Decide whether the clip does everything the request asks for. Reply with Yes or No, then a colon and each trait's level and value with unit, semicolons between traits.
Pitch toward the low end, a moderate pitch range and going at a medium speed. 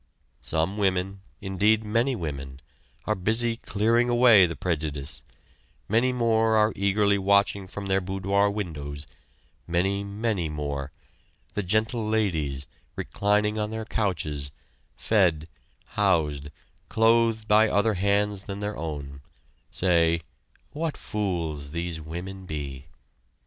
No: low, 100 Hz; average, 4.9 semitones; slow, 115 wpm